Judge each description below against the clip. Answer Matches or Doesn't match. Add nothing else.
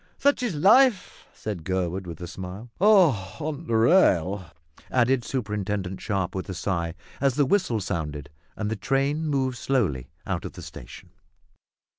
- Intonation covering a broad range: Matches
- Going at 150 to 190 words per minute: Matches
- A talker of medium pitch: Doesn't match